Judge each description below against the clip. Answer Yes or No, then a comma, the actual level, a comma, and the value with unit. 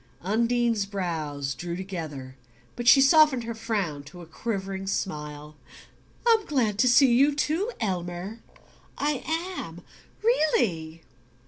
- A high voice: Yes, high, 200 Hz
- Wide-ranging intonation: Yes, wide, 6.8 semitones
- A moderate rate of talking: No, slow, 120 wpm